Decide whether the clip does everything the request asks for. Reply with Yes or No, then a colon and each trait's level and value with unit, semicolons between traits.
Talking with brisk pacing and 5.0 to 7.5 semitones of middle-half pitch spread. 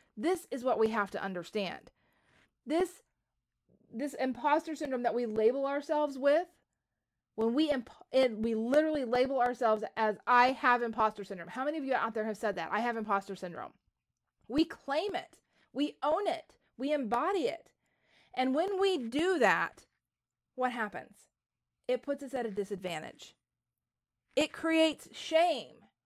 No: average, 155 wpm; average, 5.3 semitones